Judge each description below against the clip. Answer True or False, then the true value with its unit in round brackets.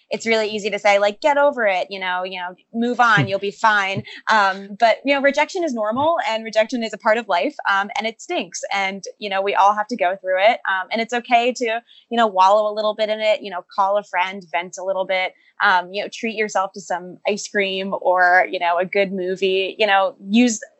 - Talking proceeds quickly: True (250 wpm)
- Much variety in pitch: False (3.3 semitones)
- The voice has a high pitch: True (205 Hz)